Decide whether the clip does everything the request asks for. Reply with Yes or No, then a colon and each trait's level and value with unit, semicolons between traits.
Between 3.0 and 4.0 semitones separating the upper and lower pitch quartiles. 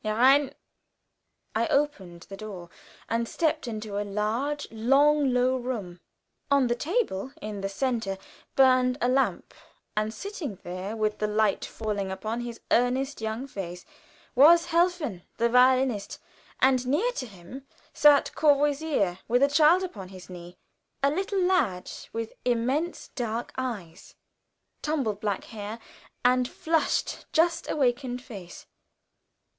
No: average, 5.1 semitones